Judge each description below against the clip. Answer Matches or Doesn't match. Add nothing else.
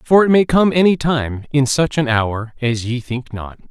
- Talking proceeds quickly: Matches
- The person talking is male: Matches